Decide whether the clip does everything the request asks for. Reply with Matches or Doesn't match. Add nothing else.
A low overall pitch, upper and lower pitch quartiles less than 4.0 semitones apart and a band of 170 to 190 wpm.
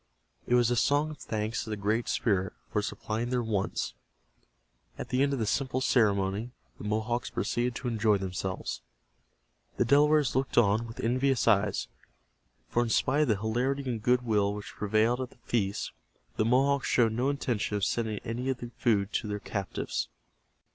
Matches